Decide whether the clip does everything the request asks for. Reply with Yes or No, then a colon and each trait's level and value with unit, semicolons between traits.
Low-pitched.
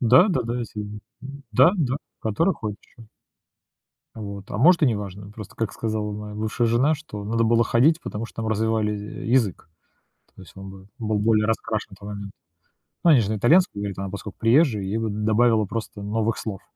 Yes: low, 110 Hz